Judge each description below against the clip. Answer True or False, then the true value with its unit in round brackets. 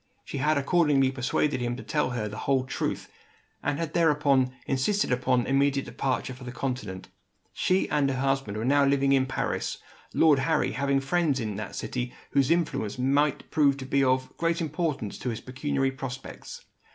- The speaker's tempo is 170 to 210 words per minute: True (180 wpm)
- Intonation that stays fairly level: True (2.3 semitones)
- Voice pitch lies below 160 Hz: True (135 Hz)